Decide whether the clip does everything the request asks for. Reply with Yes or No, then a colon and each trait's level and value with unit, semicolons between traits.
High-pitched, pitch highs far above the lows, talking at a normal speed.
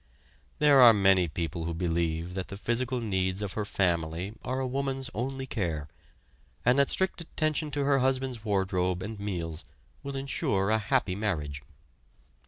No: low, 105 Hz; wide, 6.7 semitones; average, 160 wpm